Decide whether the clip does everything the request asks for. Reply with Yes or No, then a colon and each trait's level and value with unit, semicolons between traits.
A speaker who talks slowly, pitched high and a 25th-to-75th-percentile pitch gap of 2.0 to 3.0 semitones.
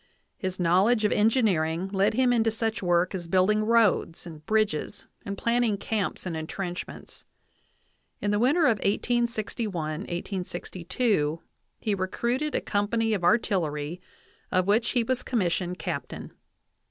No: slow, 130 wpm; high, 200 Hz; average, 4.3 semitones